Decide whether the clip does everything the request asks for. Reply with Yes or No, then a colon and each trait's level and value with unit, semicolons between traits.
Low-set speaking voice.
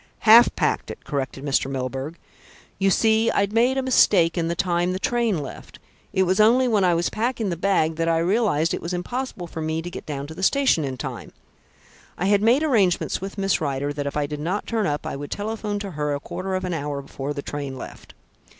No: medium, 175 Hz